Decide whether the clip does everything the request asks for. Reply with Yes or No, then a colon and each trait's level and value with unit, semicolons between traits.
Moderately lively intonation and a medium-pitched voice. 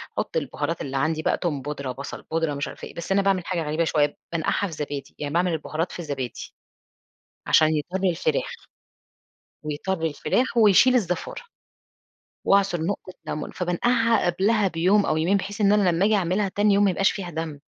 Yes: average, 4.2 semitones; medium, 175 Hz